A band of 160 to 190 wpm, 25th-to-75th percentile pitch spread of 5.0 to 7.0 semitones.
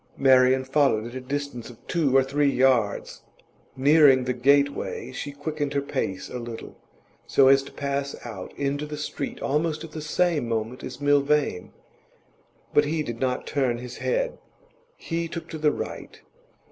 No: average, 165 wpm; average, 2.7 semitones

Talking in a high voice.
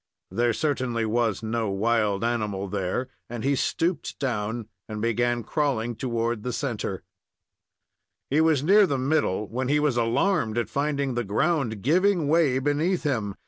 No: low, 120 Hz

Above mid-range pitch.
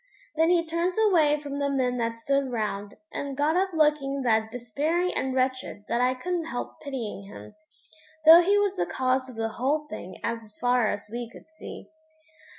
Yes: very high, 265 Hz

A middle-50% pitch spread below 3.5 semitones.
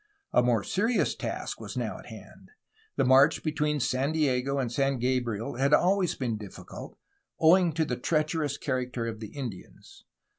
No: average, 3.9 semitones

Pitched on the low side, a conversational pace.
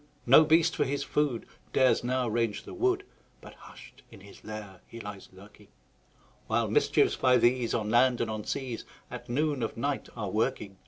Yes: low, 120 Hz; average, 190 wpm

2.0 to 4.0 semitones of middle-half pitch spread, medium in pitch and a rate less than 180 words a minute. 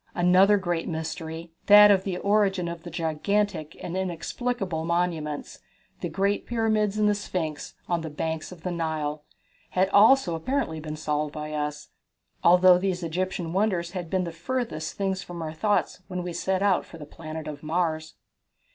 Yes: average, 3.5 semitones; medium, 175 Hz; average, 165 wpm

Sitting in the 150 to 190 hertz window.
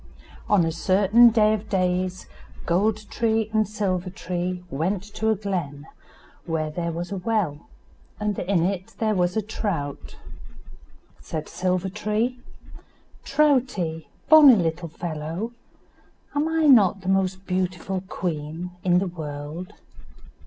Yes: medium, 185 Hz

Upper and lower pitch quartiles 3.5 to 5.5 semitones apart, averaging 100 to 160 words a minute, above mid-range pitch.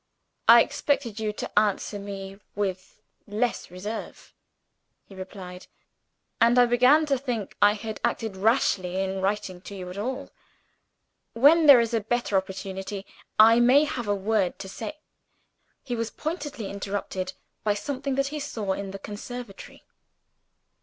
Yes: average, 4.1 semitones; average, 150 wpm; high, 215 Hz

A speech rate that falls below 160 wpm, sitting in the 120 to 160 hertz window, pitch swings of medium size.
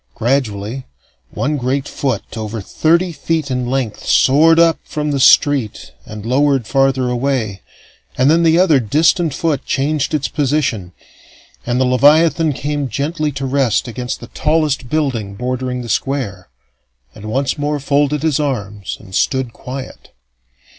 Yes: average, 145 wpm; low, 135 Hz; average, 3.5 semitones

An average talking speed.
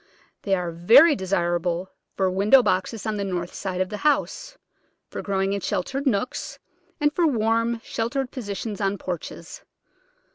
Yes: average, 150 wpm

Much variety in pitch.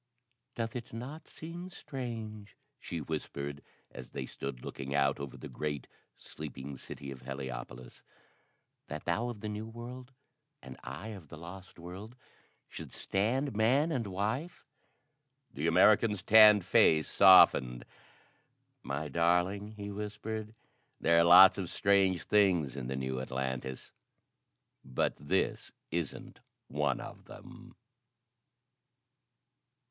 Yes: wide, 7.6 semitones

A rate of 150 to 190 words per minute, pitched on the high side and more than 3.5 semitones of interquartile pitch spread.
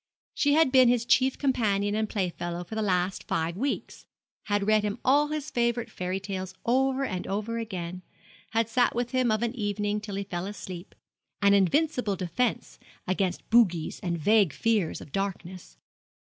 Yes: average, 170 wpm; high, 210 Hz; average, 4.4 semitones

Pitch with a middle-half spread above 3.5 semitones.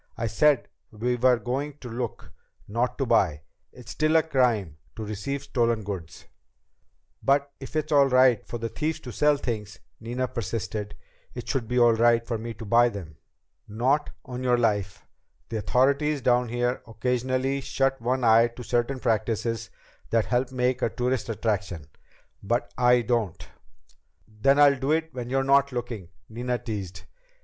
No: average, 3.0 semitones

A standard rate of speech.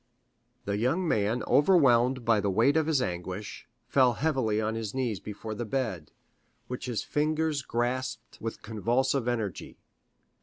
Yes: average, 145 wpm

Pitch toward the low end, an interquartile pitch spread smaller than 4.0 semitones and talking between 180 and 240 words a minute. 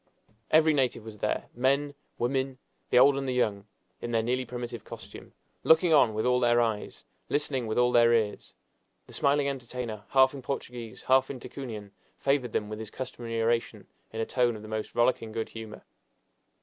Yes: low, 120 Hz; average, 2.9 semitones; average, 185 wpm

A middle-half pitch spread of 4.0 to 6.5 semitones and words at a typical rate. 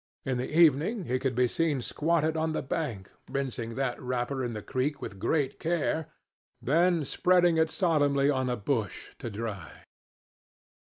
Yes: average, 4.6 semitones; average, 160 wpm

